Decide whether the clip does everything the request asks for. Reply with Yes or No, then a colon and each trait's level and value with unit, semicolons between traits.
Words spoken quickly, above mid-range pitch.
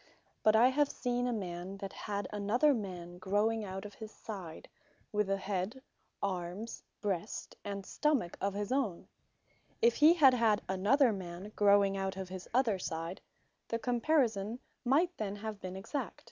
No: average, 160 wpm; high, 205 Hz